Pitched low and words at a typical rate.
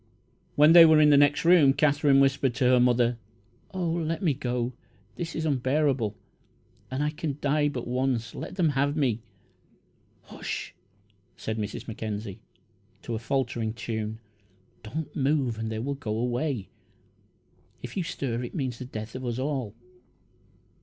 Yes: low, 130 Hz; average, 155 wpm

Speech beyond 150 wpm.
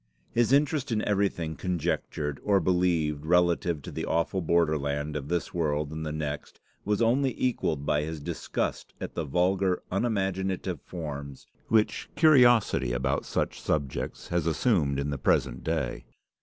No: average, 145 wpm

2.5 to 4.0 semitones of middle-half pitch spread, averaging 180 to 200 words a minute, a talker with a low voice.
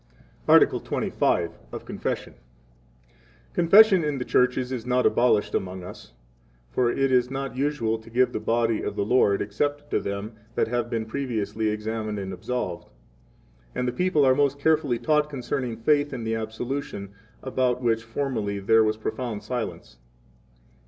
No: average, 3.7 semitones; average, 165 wpm; low, 120 Hz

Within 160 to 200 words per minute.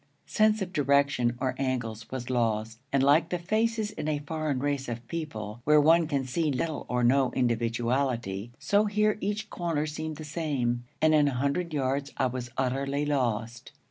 Yes: average, 175 wpm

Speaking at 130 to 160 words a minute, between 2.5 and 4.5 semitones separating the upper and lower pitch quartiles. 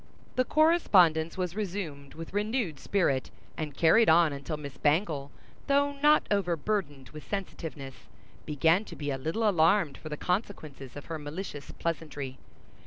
No: average, 145 wpm; wide, 5.5 semitones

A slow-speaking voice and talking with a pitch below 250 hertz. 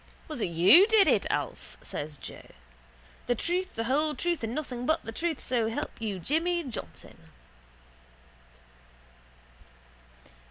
No: slow, 130 wpm; very high, 260 Hz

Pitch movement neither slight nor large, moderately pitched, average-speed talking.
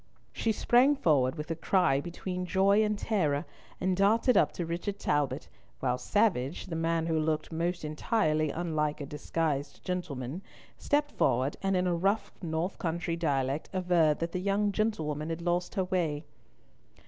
Yes: average, 4.0 semitones; medium, 170 Hz; average, 160 wpm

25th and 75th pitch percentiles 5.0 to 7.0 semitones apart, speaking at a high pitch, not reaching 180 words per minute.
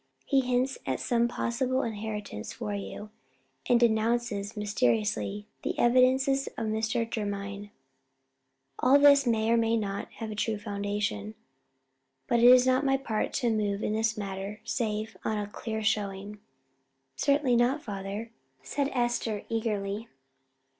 No: average, 2.9 semitones; high, 220 Hz; average, 140 wpm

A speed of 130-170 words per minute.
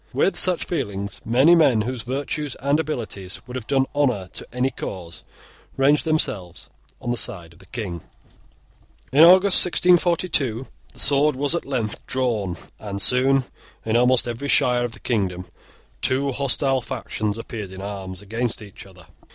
Yes: average, 160 wpm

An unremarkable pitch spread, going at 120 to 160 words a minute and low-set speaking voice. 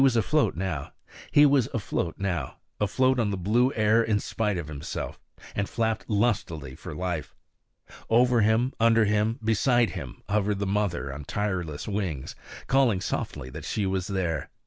Yes: average, 4.2 semitones; average, 145 wpm; low, 105 Hz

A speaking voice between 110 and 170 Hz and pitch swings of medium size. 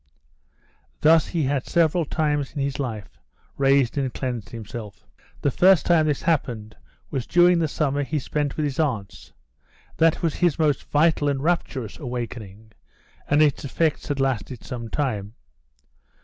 Yes: medium, 140 Hz; average, 4.1 semitones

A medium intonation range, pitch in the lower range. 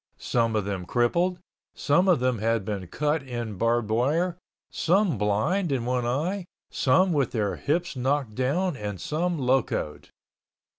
No: wide, 6.7 semitones; low, 130 Hz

